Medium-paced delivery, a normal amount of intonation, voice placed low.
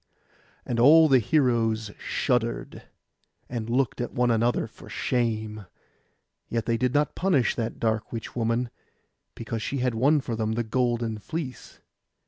No: average, 150 wpm; narrow, 2.1 semitones; low, 120 Hz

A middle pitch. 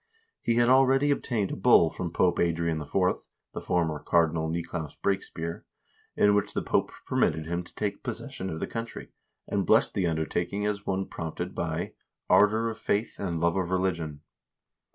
No: very low, 90 Hz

